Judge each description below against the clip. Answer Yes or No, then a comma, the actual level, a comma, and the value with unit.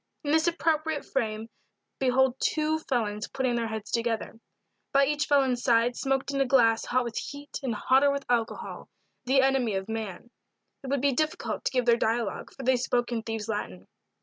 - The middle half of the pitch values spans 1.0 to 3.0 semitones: No, average, 3.4 semitones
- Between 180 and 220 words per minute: Yes, average, 185 wpm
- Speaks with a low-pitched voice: No, very high, 250 Hz